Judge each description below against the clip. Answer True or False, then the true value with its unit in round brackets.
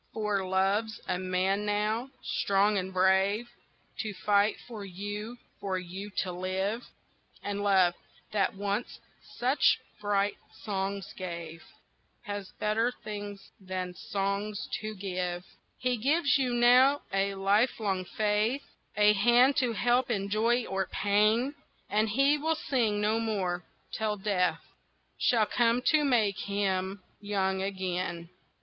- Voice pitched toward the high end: True (205 Hz)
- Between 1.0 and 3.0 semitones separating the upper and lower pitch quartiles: True (2.7 semitones)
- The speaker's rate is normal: False (130 wpm)